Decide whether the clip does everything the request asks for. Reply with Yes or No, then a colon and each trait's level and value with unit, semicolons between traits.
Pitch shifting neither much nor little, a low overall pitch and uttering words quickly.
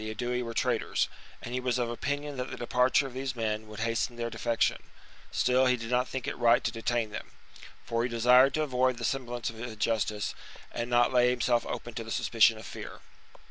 No: narrow, 1.7 semitones; low, 120 Hz; fast, 215 wpm